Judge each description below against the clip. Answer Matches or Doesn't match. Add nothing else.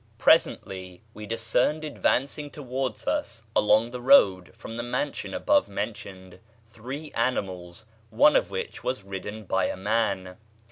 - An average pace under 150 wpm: Matches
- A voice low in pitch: Matches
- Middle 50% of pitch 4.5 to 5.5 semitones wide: Matches